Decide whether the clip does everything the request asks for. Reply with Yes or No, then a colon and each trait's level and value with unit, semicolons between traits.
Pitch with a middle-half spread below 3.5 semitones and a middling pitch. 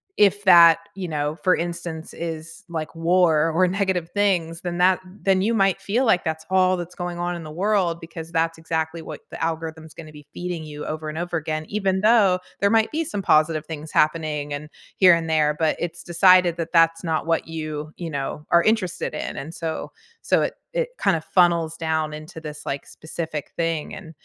Yes: narrow, 2.5 semitones; medium, 165 Hz